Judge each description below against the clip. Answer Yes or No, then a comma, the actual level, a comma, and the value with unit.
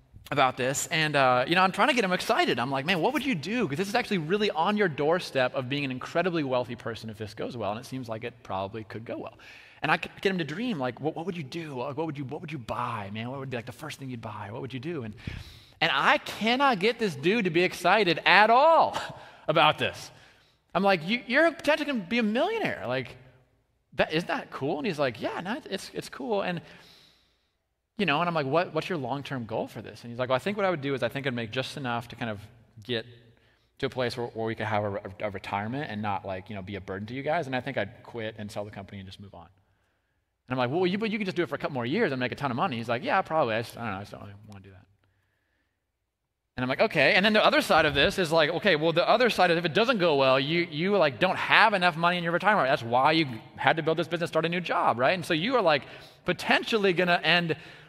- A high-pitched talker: No, low, 135 Hz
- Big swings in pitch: Yes, wide, 7.4 semitones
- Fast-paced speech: Yes, fast, 290 wpm